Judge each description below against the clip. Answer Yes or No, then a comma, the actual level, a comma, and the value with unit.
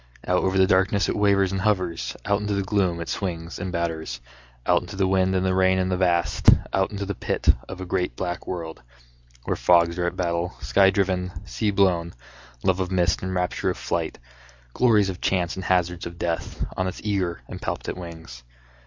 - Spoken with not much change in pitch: Yes, narrow, 1.8 semitones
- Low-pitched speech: Yes, very low, 95 Hz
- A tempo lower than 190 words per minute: No, fast, 205 wpm